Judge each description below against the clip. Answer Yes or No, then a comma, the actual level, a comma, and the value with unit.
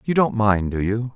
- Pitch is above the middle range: No, low, 110 Hz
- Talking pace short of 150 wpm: No, fast, 260 wpm